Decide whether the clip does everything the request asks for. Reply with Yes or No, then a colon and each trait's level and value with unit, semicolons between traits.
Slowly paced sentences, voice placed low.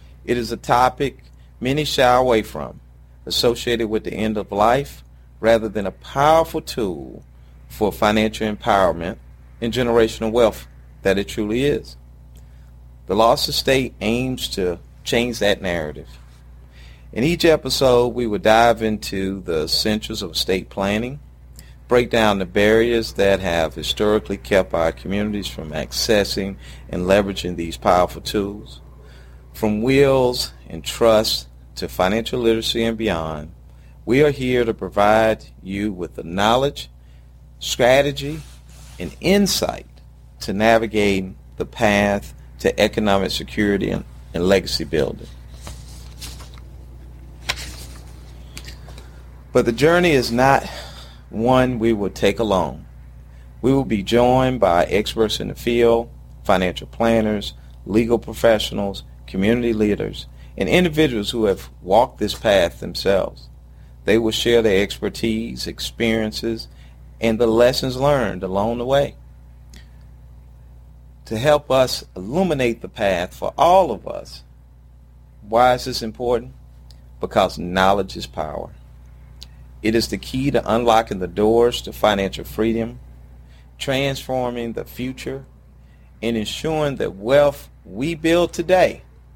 Yes: slow, 125 wpm; low, 100 Hz